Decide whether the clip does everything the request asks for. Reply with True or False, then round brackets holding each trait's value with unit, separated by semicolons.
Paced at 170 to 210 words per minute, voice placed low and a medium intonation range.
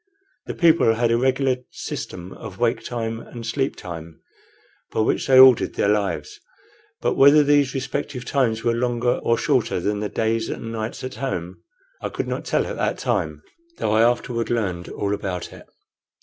True (180 wpm; 115 Hz; 3.7 semitones)